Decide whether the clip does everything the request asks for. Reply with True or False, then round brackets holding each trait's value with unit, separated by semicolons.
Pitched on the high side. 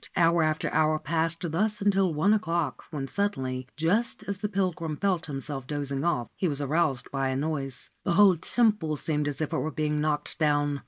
False (155 Hz)